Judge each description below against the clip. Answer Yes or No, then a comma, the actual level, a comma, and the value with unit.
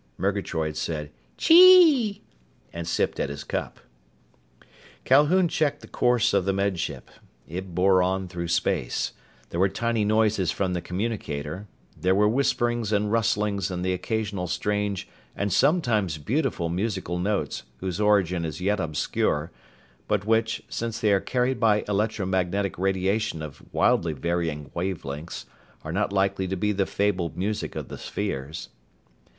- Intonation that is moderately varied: Yes, average, 3.7 semitones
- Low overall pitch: Yes, very low, 95 Hz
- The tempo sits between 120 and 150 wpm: Yes, average, 145 wpm